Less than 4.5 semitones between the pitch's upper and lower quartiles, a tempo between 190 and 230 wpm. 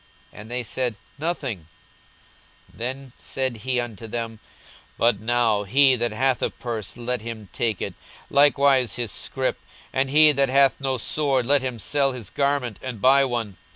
No: average, 3.1 semitones; average, 170 wpm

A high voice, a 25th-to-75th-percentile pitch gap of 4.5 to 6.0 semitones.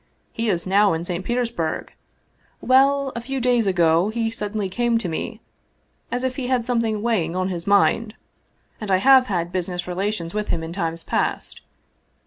Yes: high, 210 Hz; average, 5.1 semitones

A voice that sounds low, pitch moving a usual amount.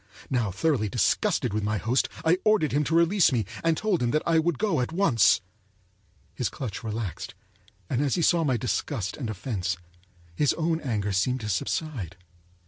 No: low, 130 Hz; wide, 7.3 semitones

